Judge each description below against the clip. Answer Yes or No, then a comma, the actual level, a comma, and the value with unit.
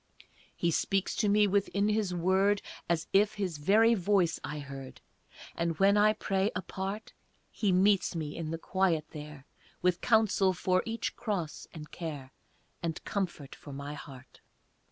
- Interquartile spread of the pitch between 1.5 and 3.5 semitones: No, average, 4.3 semitones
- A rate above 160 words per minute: No, average, 155 wpm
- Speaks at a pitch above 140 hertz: Yes, medium, 185 Hz